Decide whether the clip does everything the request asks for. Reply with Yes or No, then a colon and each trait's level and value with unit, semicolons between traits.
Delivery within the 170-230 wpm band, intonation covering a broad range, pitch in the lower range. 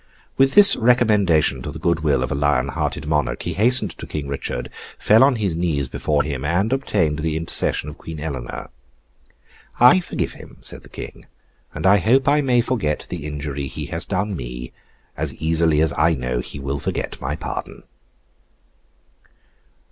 Yes: average, 175 wpm; wide, 6.7 semitones; very low, 80 Hz